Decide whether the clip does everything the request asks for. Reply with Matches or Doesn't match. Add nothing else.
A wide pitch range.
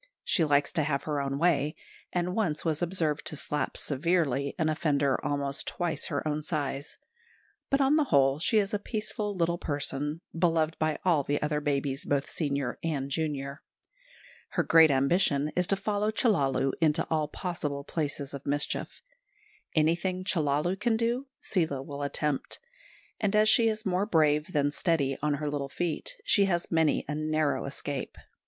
Doesn't match